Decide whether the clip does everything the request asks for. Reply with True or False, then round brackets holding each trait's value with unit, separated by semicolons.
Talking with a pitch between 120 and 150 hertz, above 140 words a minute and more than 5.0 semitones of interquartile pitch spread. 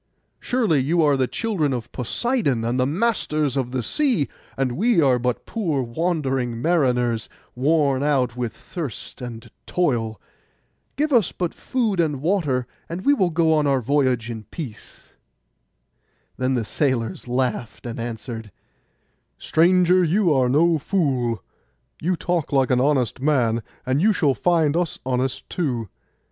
True (140 Hz; 150 wpm; 5.6 semitones)